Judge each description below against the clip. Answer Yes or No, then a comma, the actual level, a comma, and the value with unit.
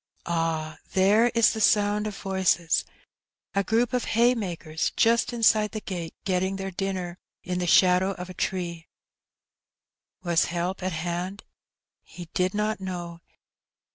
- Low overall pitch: No, medium, 185 Hz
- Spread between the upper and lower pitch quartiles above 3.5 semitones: No, average, 3.2 semitones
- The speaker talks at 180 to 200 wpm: No, average, 140 wpm